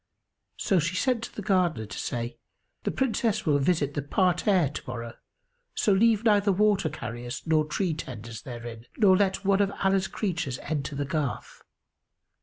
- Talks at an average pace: Yes, average, 165 wpm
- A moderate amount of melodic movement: No, wide, 6.7 semitones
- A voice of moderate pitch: Yes, medium, 170 Hz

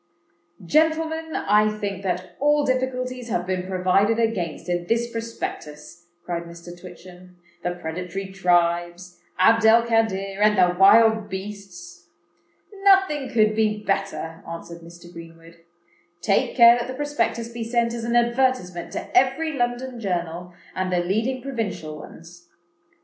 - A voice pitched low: No, high, 195 Hz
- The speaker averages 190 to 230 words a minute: No, slow, 135 wpm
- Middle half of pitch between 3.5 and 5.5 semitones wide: Yes, average, 5.1 semitones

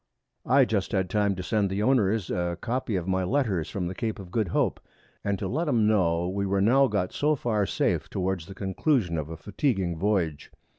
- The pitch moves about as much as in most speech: Yes, average, 3.7 semitones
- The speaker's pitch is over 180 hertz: No, low, 100 Hz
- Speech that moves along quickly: Yes, fast, 210 wpm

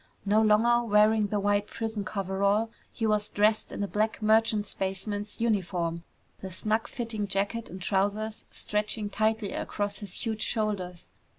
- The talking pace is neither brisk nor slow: Yes, average, 150 wpm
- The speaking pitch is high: Yes, high, 210 Hz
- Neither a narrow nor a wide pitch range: No, narrow, 1.6 semitones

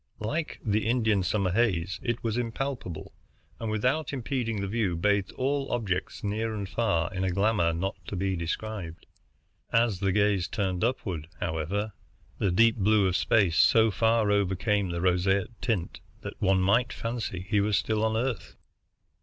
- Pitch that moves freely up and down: No, average, 3.4 semitones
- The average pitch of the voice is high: No, low, 105 Hz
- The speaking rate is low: No, average, 160 wpm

